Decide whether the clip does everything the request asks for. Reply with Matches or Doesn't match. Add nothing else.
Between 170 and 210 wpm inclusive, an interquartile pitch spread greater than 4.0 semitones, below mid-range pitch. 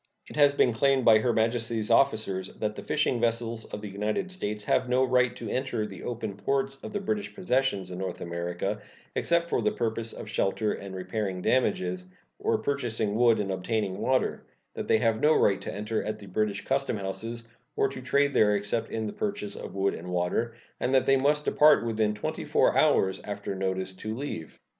Matches